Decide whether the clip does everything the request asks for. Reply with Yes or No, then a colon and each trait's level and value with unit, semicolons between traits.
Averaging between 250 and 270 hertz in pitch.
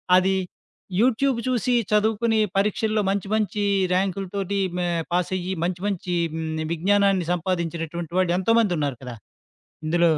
No: high, 190 Hz